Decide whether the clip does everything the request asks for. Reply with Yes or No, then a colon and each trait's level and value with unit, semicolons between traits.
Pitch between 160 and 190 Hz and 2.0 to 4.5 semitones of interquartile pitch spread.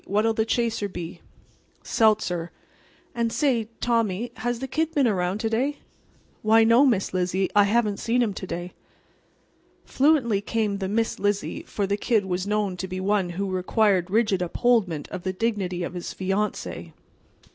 No: high, 210 Hz; average, 3.6 semitones